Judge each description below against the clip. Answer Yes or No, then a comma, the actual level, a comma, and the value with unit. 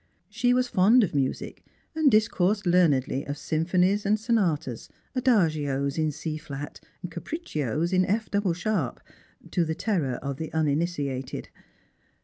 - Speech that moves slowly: Yes, slow, 130 wpm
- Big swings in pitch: Yes, wide, 6.3 semitones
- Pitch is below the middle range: No, medium, 175 Hz